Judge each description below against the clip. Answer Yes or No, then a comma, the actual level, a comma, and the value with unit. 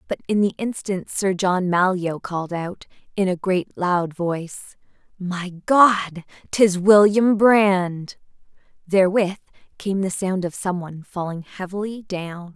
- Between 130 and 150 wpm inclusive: Yes, average, 140 wpm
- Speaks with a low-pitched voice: No, medium, 185 Hz